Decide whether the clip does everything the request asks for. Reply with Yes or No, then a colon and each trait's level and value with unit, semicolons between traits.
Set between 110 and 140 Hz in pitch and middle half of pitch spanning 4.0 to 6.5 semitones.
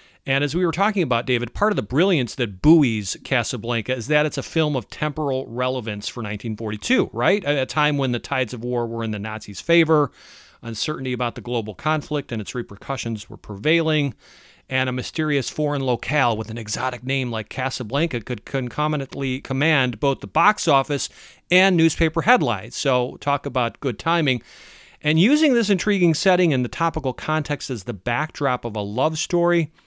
Yes: low, 135 Hz; average, 4.4 semitones